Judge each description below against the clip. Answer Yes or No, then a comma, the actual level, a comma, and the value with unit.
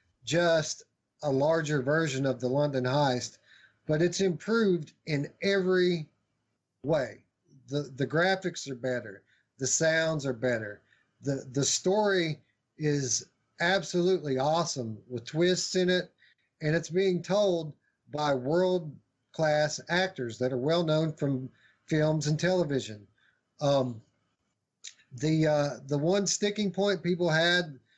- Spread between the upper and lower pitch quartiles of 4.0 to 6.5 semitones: Yes, average, 5.1 semitones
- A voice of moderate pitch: Yes, medium, 150 Hz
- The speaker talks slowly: Yes, slow, 125 wpm